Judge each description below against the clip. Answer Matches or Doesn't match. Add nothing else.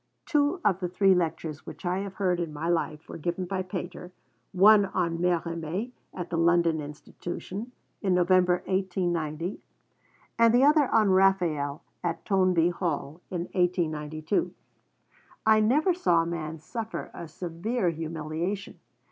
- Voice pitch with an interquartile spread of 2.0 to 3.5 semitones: Matches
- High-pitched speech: Doesn't match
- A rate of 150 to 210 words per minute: Doesn't match